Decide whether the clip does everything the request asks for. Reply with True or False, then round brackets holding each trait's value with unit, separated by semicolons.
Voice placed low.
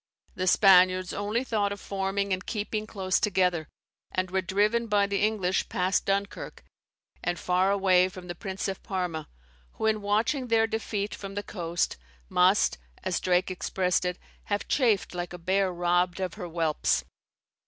False (190 Hz)